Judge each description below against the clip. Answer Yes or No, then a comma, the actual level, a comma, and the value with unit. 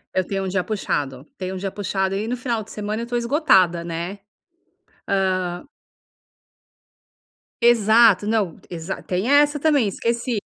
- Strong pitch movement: No, average, 4.1 semitones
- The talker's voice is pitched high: Yes, high, 205 Hz